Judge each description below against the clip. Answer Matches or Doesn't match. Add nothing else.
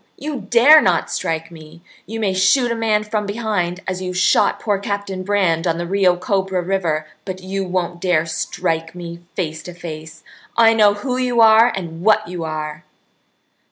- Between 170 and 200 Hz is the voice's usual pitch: Matches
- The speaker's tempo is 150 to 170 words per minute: Doesn't match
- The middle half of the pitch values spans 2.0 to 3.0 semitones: Doesn't match